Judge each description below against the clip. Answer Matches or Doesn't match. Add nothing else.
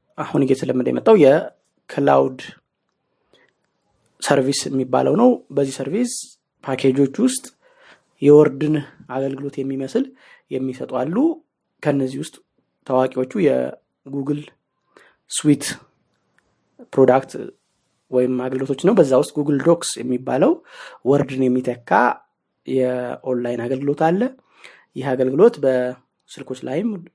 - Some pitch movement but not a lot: Matches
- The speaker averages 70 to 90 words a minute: Matches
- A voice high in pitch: Doesn't match